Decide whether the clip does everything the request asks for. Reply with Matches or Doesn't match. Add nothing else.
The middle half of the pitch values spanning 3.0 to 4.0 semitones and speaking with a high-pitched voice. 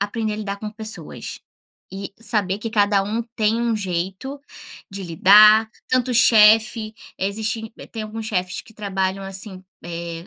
Doesn't match